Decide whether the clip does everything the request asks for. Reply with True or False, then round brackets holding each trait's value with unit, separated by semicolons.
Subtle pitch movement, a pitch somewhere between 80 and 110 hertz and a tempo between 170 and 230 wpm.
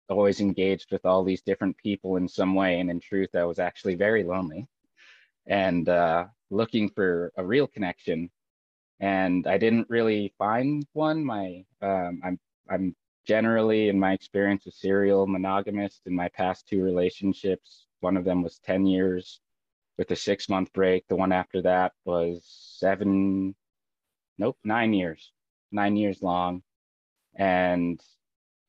False (1.9 semitones; 95 Hz; 145 wpm)